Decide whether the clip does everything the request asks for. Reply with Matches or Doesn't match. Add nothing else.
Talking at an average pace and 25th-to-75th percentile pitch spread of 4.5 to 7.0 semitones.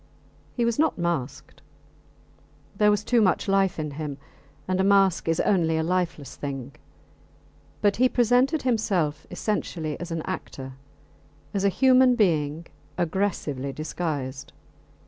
Doesn't match